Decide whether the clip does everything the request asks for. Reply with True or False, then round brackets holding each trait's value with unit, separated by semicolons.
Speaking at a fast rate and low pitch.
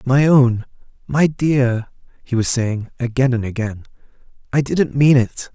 False (150 wpm; 125 Hz)